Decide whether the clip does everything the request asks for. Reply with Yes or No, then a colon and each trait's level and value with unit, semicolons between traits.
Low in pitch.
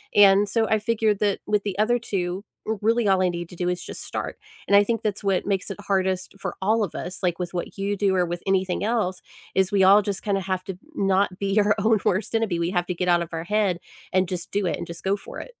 No: high, 195 Hz